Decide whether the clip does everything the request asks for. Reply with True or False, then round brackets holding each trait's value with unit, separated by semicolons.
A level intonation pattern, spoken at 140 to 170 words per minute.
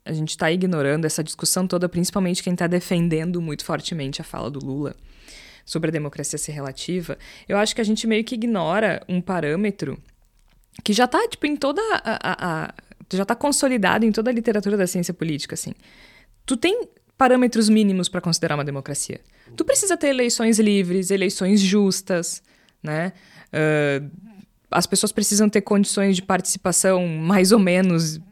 False (4.8 semitones; 165 wpm)